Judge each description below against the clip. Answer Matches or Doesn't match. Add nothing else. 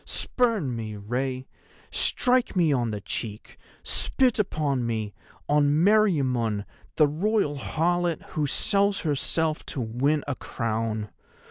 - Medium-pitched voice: Matches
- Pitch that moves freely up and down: Matches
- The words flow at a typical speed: Doesn't match